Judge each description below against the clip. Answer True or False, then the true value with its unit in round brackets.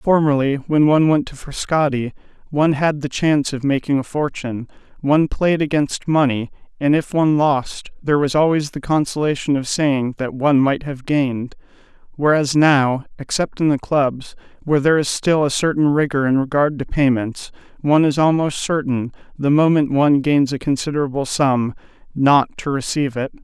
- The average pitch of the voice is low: False (145 Hz)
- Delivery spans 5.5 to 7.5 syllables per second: False (5.3 syllables/s)